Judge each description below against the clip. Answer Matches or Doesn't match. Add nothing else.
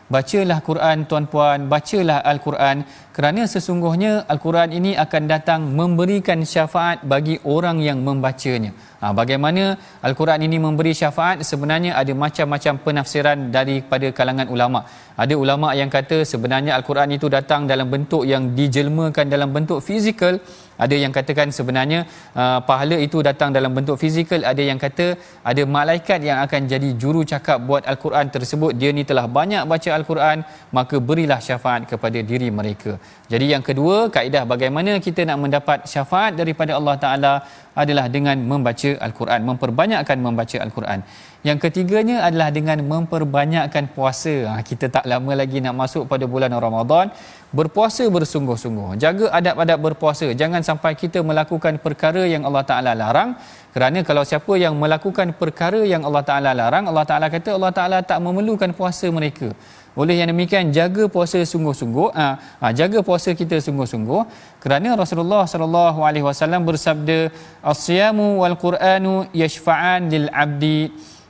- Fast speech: Matches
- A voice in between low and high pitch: Matches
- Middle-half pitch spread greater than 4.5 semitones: Doesn't match